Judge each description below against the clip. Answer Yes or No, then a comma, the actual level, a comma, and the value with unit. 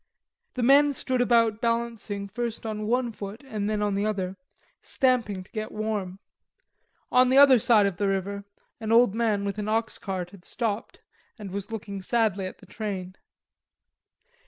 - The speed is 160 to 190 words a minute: Yes, average, 165 wpm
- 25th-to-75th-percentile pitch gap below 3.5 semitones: Yes, average, 2.8 semitones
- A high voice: Yes, high, 215 Hz